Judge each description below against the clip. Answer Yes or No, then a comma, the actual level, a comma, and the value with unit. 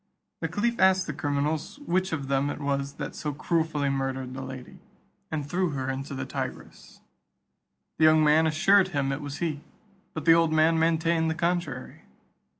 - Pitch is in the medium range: Yes, medium, 155 Hz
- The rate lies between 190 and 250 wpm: No, average, 175 wpm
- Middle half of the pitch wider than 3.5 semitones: No, average, 3.1 semitones